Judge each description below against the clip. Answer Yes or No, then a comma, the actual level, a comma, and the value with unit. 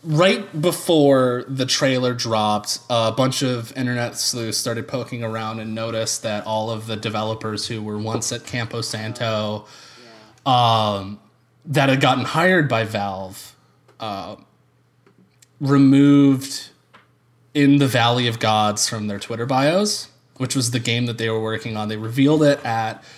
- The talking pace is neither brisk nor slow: Yes, average, 150 wpm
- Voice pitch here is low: Yes, low, 120 Hz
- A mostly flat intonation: No, average, 3.3 semitones